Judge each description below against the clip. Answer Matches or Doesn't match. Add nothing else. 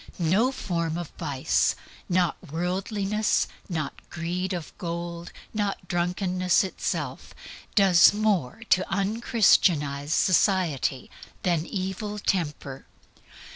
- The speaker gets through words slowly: Matches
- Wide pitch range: Doesn't match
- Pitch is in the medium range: Matches